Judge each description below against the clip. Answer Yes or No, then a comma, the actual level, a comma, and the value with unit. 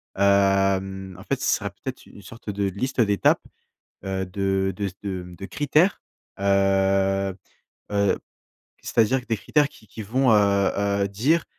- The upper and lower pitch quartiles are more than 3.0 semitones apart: No, narrow, 2.5 semitones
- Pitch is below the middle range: Yes, low, 100 Hz